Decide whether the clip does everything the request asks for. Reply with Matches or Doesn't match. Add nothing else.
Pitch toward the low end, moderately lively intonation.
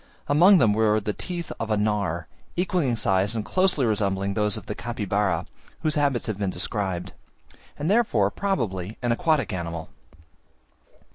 Doesn't match